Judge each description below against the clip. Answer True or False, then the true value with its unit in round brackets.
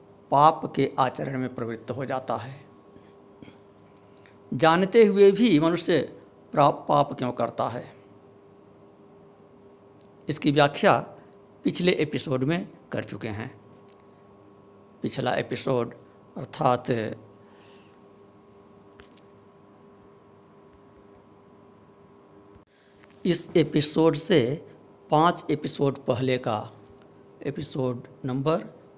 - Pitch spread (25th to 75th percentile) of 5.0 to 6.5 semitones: True (5.5 semitones)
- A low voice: True (100 Hz)